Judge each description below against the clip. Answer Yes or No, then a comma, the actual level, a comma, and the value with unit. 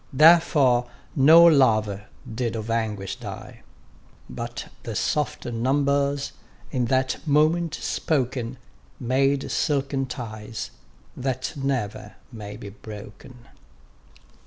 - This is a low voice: Yes, low, 130 Hz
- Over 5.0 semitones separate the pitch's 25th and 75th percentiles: No, average, 3.9 semitones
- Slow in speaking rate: Yes, slow, 95 wpm